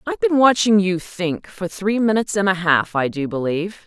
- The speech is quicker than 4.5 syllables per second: Yes, 5.4 syllables/s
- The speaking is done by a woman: Yes, female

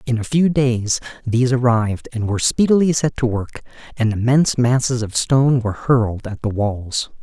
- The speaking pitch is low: Yes, low, 120 Hz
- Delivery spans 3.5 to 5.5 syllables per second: Yes, 5.4 syllables/s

